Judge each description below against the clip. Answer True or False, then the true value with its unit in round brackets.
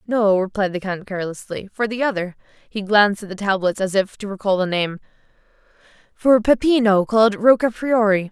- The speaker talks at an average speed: True (175 wpm)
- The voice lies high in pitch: True (205 Hz)